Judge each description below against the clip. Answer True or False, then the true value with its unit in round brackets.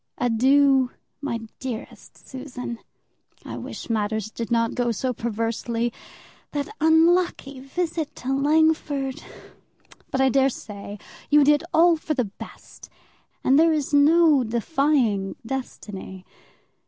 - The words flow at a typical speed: False (115 wpm)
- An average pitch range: True (4.4 semitones)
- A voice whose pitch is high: True (265 Hz)